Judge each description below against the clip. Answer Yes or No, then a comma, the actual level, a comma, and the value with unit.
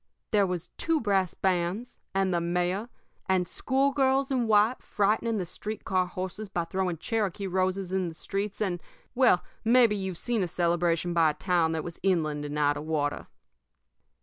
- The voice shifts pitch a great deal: No, average, 3.7 semitones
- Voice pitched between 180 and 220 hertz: Yes, medium, 185 Hz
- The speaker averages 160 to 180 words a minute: Yes, average, 175 wpm